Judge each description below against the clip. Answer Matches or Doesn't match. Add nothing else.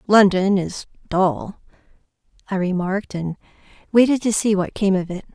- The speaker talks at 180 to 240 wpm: Doesn't match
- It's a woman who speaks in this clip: Matches